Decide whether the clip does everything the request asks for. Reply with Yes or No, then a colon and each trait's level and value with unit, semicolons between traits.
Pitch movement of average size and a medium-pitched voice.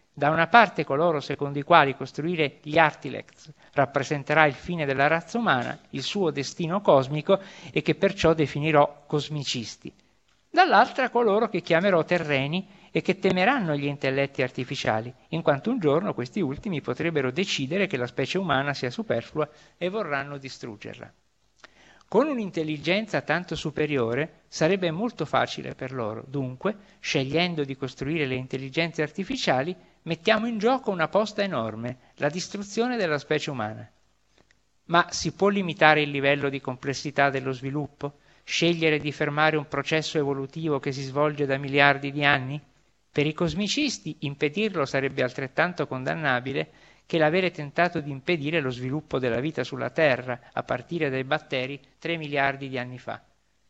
Yes: average, 3.8 semitones; medium, 150 Hz